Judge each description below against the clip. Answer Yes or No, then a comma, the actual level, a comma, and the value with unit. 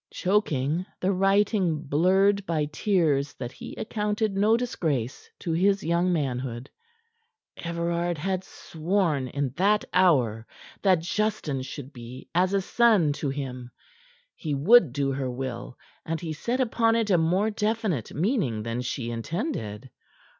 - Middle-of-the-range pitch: Yes, medium, 170 Hz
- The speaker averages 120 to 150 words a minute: Yes, average, 140 wpm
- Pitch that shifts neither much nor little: No, wide, 6.6 semitones